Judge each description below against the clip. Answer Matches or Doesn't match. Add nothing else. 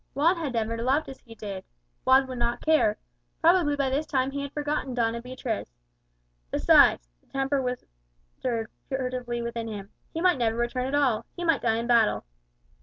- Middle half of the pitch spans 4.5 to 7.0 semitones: Doesn't match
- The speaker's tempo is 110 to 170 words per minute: Doesn't match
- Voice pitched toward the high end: Matches